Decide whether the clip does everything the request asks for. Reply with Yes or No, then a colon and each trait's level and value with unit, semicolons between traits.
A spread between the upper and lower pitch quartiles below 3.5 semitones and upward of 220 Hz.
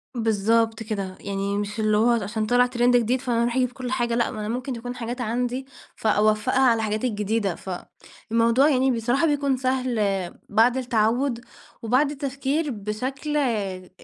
Yes: average, 3.0 semitones; high, 235 Hz